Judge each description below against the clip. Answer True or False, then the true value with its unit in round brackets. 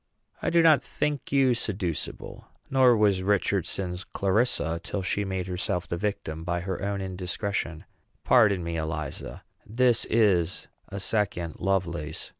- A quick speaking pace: False (135 wpm)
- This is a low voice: True (95 Hz)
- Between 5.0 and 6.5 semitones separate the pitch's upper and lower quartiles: False (3.5 semitones)